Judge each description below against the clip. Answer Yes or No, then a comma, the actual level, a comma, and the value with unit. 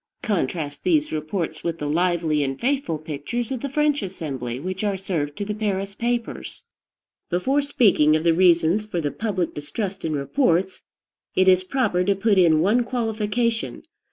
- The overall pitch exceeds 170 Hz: Yes, medium, 185 Hz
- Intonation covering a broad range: Yes, wide, 6.0 semitones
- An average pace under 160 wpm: No, average, 165 wpm